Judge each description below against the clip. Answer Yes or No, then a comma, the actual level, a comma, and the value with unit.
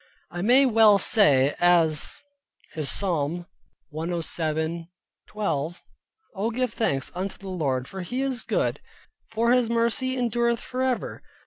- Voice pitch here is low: No, high, 195 Hz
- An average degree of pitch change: No, wide, 6.4 semitones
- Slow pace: Yes, slow, 125 wpm